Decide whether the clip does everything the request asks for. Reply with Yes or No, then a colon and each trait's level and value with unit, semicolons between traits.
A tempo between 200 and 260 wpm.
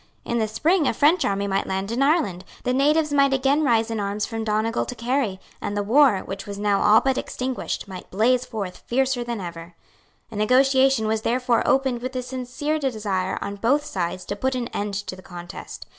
Yes: fast, 205 wpm